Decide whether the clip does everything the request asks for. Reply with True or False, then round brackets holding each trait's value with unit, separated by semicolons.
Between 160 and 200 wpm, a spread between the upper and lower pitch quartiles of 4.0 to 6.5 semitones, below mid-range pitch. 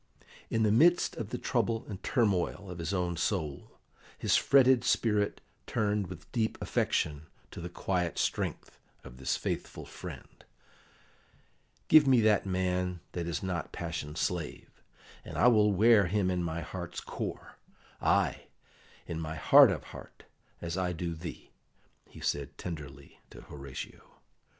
False (145 wpm; 4.3 semitones; 90 Hz)